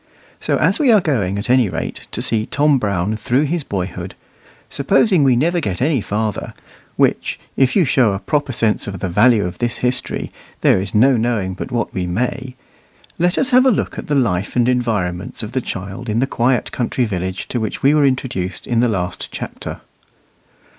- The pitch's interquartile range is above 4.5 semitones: Yes, average, 5.1 semitones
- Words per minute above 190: Yes, average, 200 wpm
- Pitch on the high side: No, low, 120 Hz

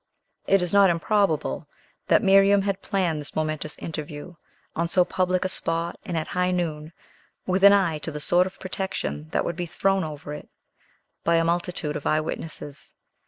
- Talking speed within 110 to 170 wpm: No, average, 180 wpm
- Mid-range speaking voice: Yes, medium, 170 Hz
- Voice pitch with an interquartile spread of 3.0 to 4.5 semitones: Yes, average, 3.4 semitones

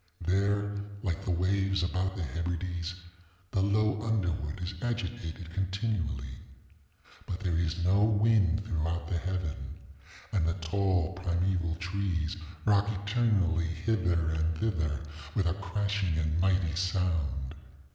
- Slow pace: Yes, slow, 125 wpm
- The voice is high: No, very low, 90 Hz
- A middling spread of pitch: Yes, average, 3.0 semitones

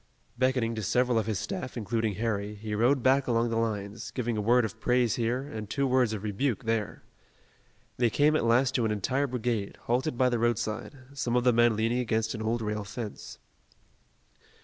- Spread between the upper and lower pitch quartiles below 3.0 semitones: Yes, narrow, 2.4 semitones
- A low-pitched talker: Yes, low, 115 Hz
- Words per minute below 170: No, average, 195 wpm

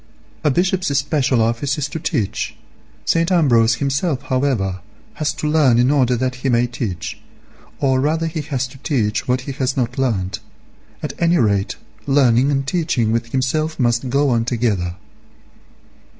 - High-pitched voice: No, low, 130 Hz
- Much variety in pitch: No, average, 3.7 semitones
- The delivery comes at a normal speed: Yes, average, 155 wpm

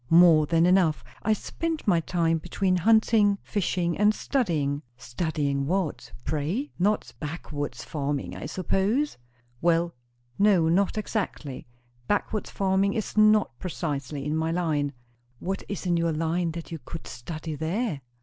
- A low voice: No, medium, 170 Hz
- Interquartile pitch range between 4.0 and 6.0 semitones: Yes, average, 4.4 semitones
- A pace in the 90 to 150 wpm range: Yes, average, 140 wpm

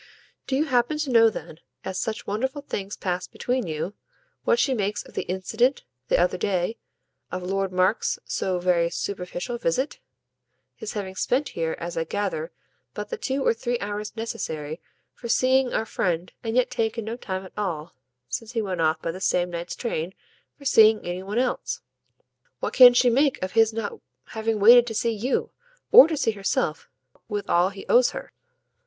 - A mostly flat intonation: No, average, 5.0 semitones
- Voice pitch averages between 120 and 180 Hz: No, high, 210 Hz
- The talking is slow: No, average, 185 wpm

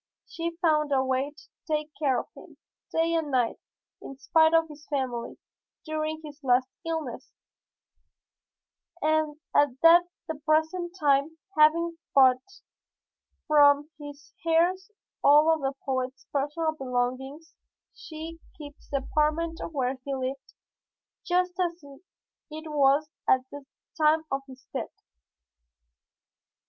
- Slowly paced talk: Yes, slow, 120 wpm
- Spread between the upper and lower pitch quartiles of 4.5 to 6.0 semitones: No, average, 3.0 semitones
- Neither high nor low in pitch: No, very high, 300 Hz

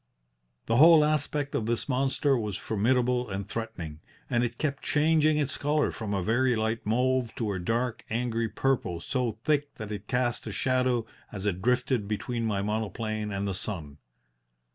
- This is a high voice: No, low, 120 Hz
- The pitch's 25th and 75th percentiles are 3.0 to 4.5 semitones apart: Yes, average, 3.6 semitones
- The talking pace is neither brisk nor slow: Yes, average, 170 wpm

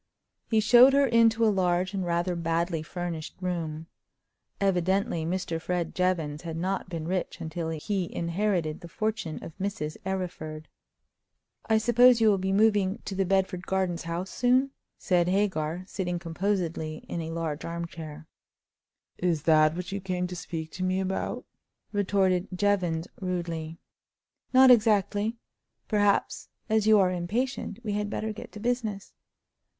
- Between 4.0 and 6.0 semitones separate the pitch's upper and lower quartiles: No, average, 3.4 semitones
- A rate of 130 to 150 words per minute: Yes, average, 145 wpm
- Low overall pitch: No, medium, 185 Hz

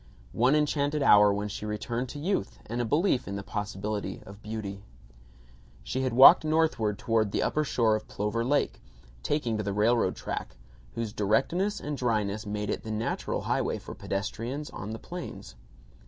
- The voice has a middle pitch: No, low, 110 Hz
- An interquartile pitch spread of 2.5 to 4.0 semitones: No, average, 4.7 semitones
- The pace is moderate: Yes, average, 170 wpm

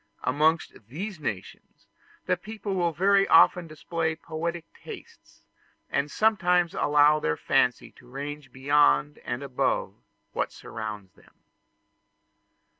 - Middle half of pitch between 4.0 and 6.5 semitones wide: Yes, average, 4.7 semitones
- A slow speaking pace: Yes, slow, 115 wpm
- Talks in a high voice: No, medium, 155 Hz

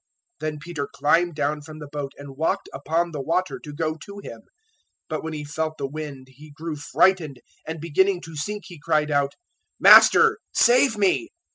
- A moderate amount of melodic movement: Yes, average, 3.0 semitones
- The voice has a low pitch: No, medium, 155 Hz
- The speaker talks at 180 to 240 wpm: Yes, average, 185 wpm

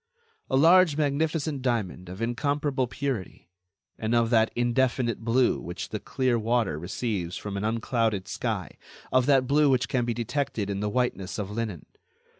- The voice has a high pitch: No, low, 120 Hz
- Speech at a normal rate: Yes, average, 160 wpm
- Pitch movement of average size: Yes, average, 4.2 semitones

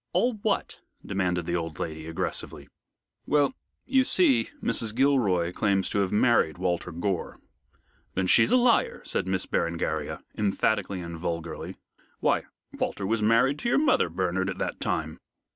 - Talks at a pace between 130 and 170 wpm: Yes, average, 150 wpm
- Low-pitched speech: Yes, very low, 95 Hz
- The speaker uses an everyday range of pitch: No, wide, 6.7 semitones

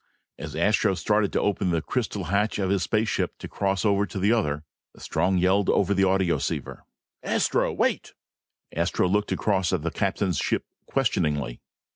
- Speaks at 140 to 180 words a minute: Yes, average, 160 wpm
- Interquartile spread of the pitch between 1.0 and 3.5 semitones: Yes, average, 2.7 semitones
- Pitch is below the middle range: Yes, very low, 95 Hz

